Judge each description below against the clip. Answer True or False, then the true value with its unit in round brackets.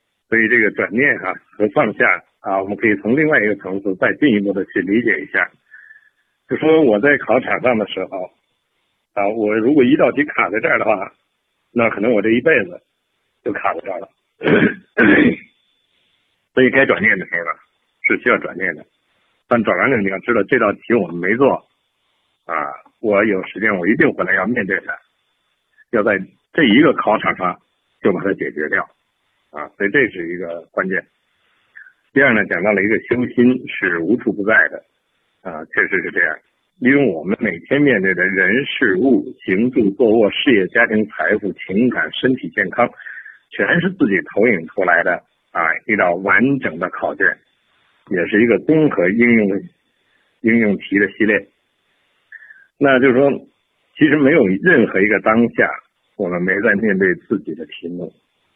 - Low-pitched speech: True (120 Hz)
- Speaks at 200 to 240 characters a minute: False (250 characters per minute)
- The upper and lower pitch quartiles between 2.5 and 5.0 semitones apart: False (5.5 semitones)